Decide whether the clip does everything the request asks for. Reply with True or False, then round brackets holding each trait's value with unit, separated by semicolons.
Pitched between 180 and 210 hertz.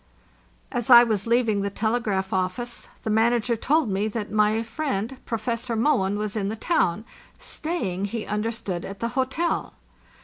False (220 Hz)